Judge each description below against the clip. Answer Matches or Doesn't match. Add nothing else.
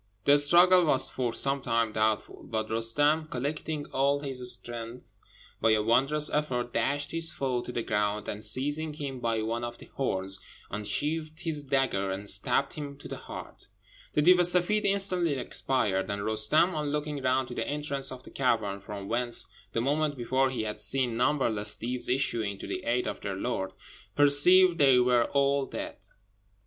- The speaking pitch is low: Matches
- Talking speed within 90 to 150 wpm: Doesn't match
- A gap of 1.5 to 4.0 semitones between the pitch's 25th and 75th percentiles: Doesn't match